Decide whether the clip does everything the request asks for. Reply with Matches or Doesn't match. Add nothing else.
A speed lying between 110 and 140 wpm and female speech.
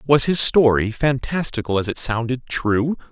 Doesn't match